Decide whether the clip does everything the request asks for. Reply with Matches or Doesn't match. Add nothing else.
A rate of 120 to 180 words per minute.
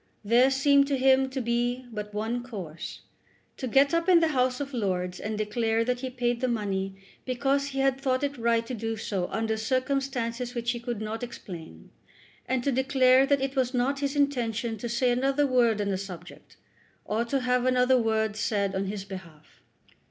Doesn't match